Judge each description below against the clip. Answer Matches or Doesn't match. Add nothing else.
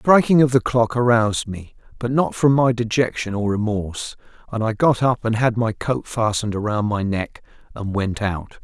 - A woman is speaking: Doesn't match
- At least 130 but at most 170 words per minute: Doesn't match